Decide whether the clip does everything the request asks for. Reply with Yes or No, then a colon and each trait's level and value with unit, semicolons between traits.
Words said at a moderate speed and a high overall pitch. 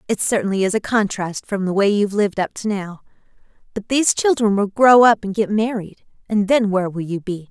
No: fast, 225 wpm; high, 205 Hz